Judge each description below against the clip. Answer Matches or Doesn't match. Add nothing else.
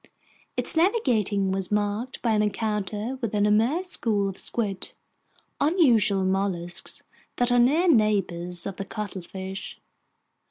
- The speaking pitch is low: Doesn't match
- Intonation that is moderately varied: Matches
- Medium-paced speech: Doesn't match